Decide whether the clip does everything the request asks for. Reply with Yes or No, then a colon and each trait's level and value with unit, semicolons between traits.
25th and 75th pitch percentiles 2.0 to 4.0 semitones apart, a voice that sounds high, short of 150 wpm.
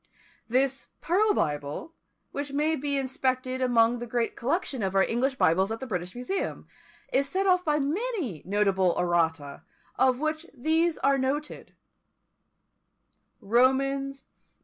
No: average, 5.0 semitones; very high, 260 Hz; slow, 135 wpm